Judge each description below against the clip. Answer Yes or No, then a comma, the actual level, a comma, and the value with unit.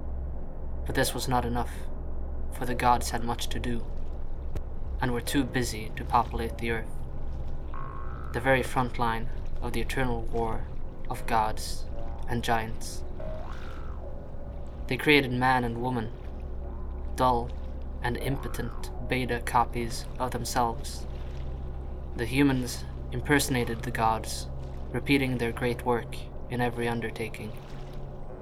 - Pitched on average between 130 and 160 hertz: No, very low, 75 Hz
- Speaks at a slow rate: Yes, slow, 120 wpm